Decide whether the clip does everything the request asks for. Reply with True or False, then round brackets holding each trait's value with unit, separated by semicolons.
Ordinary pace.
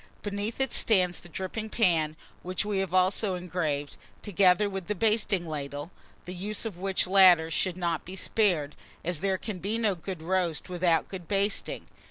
True (175 wpm)